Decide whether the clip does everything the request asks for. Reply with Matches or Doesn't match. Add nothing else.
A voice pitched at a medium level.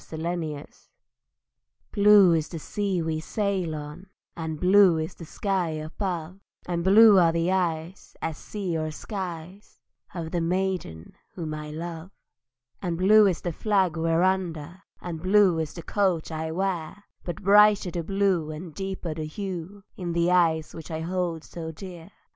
Matches